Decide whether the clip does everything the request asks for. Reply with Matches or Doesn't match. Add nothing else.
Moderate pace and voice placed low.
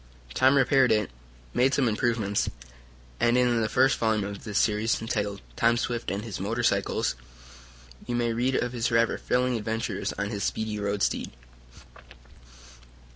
Matches